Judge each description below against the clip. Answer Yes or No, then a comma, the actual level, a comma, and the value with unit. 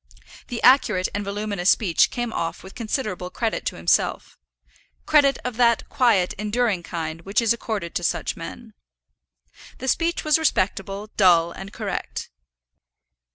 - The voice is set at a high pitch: Yes, high, 210 Hz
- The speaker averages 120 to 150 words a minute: Yes, average, 140 wpm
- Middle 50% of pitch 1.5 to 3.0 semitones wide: No, average, 4.8 semitones